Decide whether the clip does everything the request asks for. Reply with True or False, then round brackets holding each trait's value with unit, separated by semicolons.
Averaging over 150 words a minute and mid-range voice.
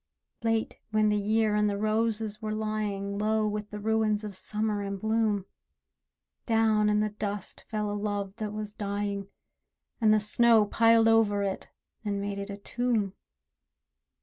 False (160 wpm; 210 Hz)